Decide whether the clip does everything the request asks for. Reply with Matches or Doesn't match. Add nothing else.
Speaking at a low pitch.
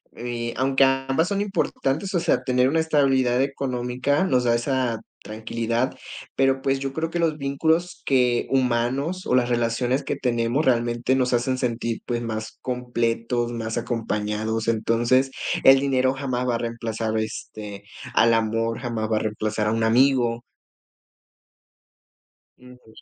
Matches